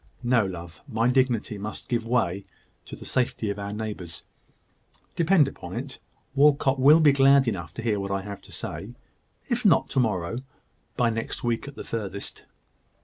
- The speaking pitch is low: Yes, low, 115 Hz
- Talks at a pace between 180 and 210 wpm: No, average, 170 wpm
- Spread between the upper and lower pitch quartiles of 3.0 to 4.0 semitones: No, average, 5.1 semitones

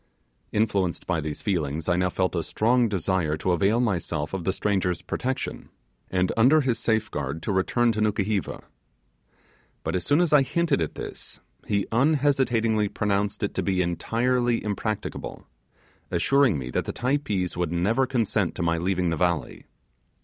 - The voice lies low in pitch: Yes, low, 100 Hz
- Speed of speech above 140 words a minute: Yes, average, 160 wpm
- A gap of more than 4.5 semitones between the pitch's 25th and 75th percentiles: Yes, average, 5.1 semitones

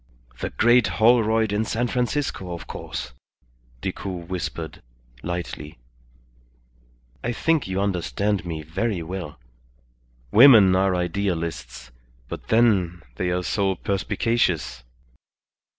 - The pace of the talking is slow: Yes, slow, 105 wpm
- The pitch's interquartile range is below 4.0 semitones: No, average, 4.5 semitones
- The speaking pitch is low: Yes, very low, 95 Hz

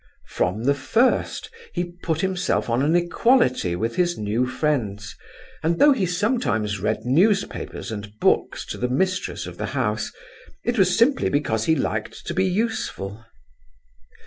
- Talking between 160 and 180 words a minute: No, average, 150 wpm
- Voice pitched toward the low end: No, medium, 155 Hz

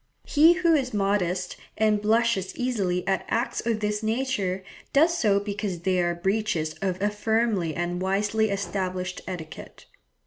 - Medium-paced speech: Yes, average, 145 wpm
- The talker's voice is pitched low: No, high, 200 Hz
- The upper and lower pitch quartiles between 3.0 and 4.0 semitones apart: Yes, average, 3.3 semitones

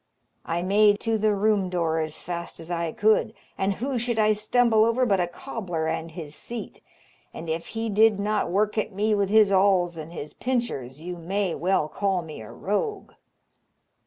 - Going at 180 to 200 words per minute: Yes, average, 185 wpm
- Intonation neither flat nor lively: Yes, average, 4.2 semitones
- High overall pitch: Yes, high, 200 Hz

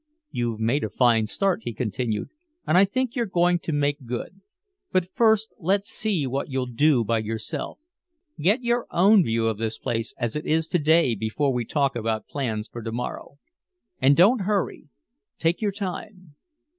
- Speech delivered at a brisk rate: No, average, 180 wpm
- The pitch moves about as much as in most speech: No, wide, 8.2 semitones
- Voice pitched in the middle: Yes, medium, 145 Hz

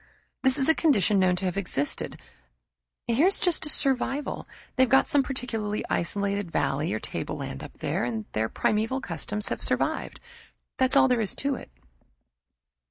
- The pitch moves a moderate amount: No, wide, 6.5 semitones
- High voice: Yes, high, 225 Hz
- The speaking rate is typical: Yes, average, 160 wpm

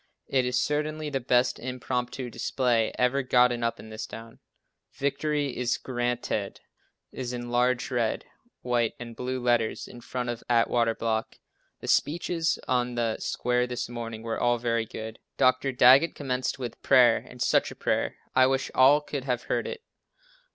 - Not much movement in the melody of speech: Yes, narrow, 1.7 semitones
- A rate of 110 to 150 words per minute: No, average, 165 wpm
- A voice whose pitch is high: No, low, 125 Hz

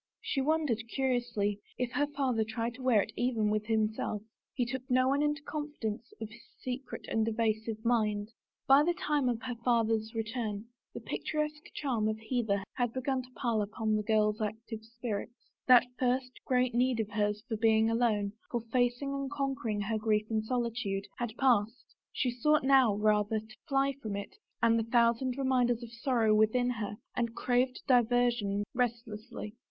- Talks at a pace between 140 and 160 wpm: No, average, 175 wpm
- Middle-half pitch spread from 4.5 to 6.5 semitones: No, average, 2.8 semitones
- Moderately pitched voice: No, high, 235 Hz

